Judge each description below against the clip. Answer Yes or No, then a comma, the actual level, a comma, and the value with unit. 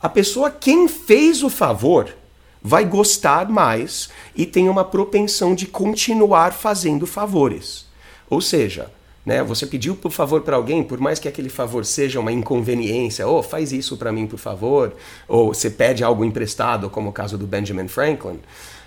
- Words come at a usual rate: Yes, average, 170 wpm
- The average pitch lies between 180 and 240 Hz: No, medium, 150 Hz